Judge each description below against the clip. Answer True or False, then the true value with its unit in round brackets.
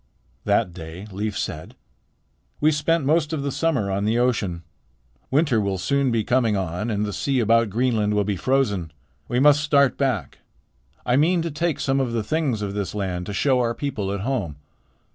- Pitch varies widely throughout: True (5.7 semitones)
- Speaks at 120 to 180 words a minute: False (195 wpm)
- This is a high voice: False (115 Hz)